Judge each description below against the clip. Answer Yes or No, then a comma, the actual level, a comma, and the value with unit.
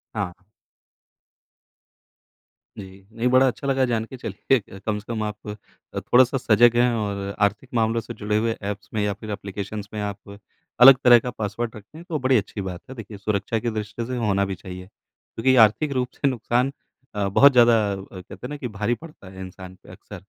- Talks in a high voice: No, low, 110 Hz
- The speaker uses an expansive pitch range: No, average, 3.5 semitones